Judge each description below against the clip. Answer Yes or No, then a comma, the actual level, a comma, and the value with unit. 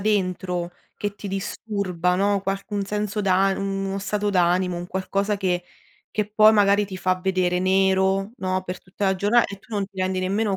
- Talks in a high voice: Yes, high, 195 Hz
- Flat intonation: Yes, narrow, 1.6 semitones